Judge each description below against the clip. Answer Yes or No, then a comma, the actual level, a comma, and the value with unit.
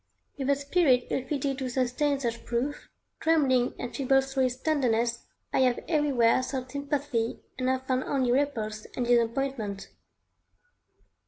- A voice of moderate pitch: No, very high, 260 Hz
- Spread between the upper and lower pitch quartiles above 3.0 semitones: No, narrow, 2.6 semitones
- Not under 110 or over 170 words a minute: Yes, average, 145 wpm